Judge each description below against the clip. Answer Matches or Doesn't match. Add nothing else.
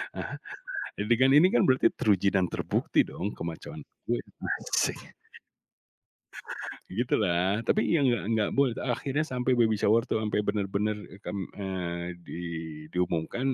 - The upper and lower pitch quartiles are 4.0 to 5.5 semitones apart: Matches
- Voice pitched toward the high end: Doesn't match